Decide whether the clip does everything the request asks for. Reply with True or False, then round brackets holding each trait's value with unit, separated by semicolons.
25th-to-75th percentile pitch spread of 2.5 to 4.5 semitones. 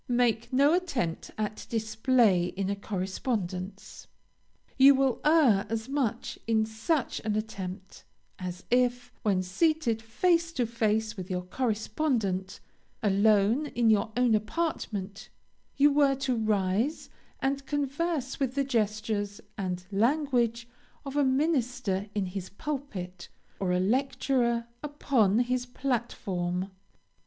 False (5.1 semitones)